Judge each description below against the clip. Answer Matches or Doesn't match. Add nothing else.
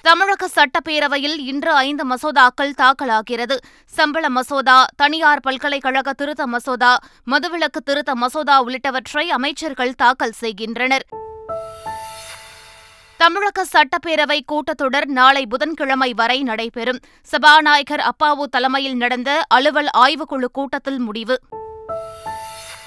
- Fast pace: Doesn't match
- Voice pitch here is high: Matches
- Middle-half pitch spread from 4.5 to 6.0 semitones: Doesn't match